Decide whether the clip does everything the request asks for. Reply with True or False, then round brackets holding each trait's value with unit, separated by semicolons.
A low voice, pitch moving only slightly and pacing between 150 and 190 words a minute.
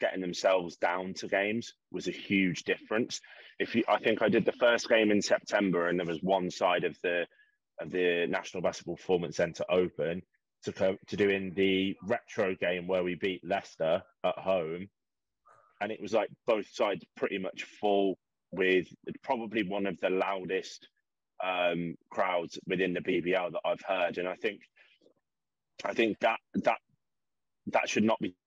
True (95 Hz; 2.1 semitones; 170 wpm)